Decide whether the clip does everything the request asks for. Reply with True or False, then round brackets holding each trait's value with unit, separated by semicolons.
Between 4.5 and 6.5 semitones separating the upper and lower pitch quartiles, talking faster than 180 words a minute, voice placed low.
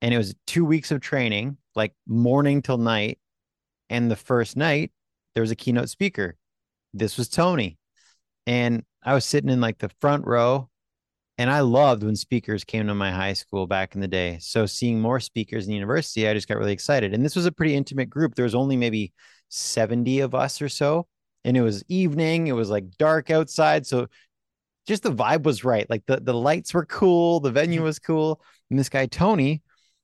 True (5.1 semitones; 205 wpm; 125 Hz)